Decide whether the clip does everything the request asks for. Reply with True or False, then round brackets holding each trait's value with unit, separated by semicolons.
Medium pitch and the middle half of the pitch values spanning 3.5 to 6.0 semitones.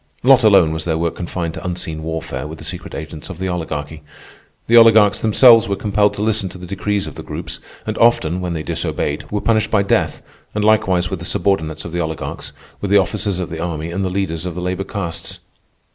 False (90 Hz; 3.9 semitones)